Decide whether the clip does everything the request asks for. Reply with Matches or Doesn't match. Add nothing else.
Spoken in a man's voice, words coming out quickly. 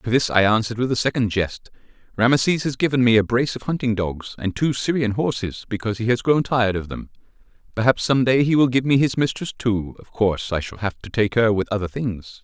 Matches